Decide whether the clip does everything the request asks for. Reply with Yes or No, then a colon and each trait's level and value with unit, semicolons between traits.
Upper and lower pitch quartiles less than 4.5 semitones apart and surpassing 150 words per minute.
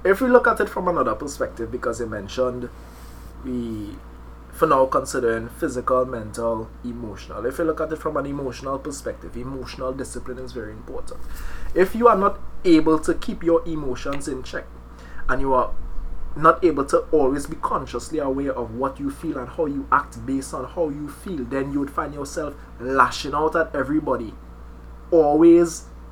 No: wide, 5.5 semitones; average, 175 wpm